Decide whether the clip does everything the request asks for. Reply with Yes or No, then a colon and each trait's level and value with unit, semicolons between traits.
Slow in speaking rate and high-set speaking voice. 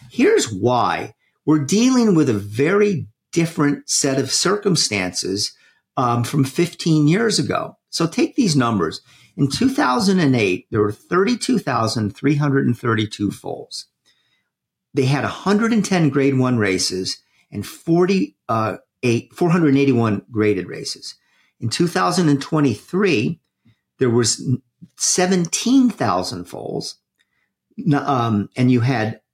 No: slow, 95 wpm; medium, 140 Hz